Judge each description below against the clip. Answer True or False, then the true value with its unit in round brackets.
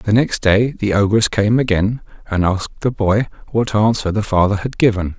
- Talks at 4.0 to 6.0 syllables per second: True (4.9 syllables/s)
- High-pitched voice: False (105 Hz)